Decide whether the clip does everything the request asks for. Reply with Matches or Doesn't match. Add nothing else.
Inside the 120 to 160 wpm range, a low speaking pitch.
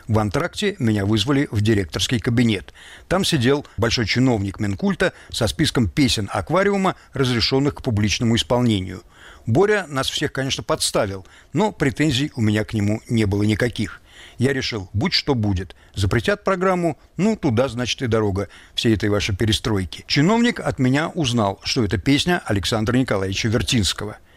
Matches